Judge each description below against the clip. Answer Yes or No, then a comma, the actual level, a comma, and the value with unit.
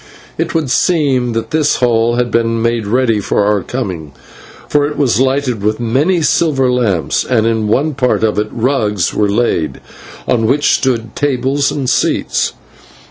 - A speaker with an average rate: Yes, average, 170 wpm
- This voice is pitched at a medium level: No, low, 120 Hz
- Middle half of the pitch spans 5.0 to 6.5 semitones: No, average, 3.6 semitones